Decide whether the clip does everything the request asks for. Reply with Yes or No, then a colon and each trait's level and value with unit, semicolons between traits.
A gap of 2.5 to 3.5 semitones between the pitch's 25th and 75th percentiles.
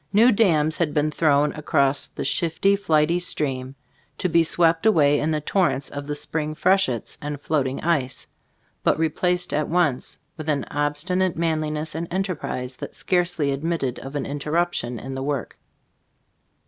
Yes: average, 3.1 semitones